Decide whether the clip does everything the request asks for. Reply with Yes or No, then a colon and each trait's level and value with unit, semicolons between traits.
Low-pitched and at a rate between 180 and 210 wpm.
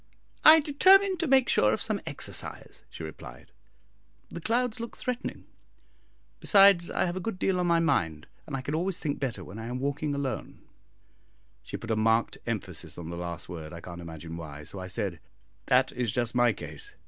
Yes: low, 120 Hz; average, 195 wpm